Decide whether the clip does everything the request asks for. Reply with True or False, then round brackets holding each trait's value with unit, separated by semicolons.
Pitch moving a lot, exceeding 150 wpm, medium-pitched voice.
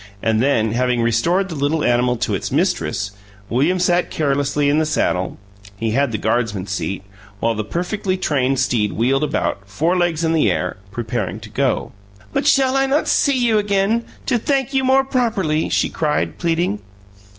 True (8.3 semitones; 175 wpm; 145 Hz)